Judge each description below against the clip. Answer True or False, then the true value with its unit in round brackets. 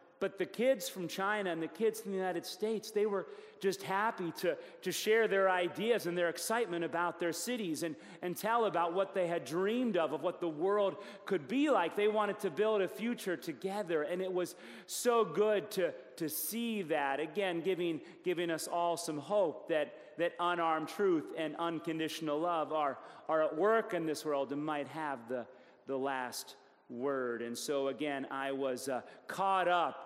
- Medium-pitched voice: True (175 Hz)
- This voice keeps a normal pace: True (190 wpm)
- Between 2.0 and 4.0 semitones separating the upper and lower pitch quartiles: False (4.4 semitones)